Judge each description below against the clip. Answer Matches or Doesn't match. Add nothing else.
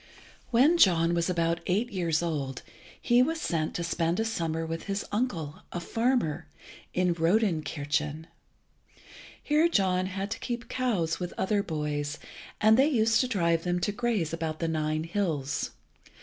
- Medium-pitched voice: Matches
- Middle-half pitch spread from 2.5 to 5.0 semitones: Doesn't match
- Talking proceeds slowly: Doesn't match